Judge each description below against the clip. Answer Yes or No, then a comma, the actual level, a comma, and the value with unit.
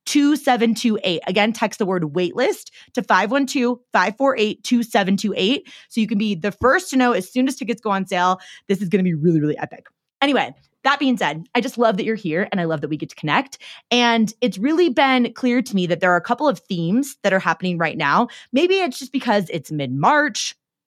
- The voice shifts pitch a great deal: Yes, wide, 5.8 semitones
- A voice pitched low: No, high, 220 Hz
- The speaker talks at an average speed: No, fast, 220 wpm